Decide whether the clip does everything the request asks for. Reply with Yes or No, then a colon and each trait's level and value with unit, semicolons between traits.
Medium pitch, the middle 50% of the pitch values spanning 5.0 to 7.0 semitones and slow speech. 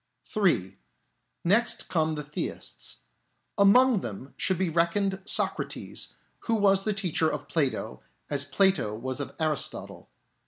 Yes: medium, 170 Hz; average, 5.3 semitones; slow, 125 wpm